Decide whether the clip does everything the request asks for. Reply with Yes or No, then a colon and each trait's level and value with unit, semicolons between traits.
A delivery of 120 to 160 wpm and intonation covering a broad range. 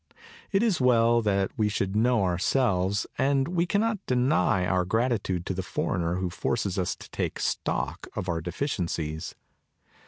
Yes: average, 155 wpm; wide, 5.9 semitones